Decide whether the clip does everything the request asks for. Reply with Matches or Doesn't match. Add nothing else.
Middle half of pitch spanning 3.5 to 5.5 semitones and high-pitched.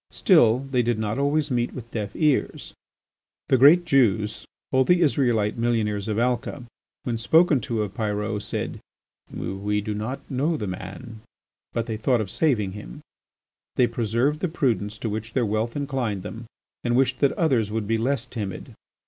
Doesn't match